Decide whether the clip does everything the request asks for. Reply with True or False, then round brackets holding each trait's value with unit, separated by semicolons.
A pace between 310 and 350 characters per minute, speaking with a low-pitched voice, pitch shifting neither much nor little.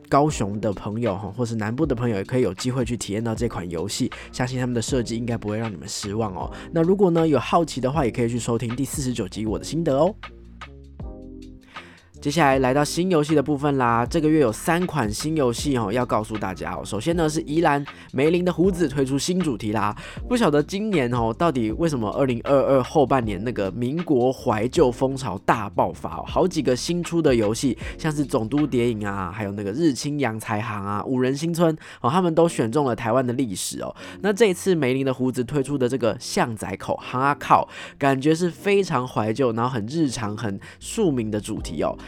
False (320 characters per minute; 125 Hz; 5.7 semitones)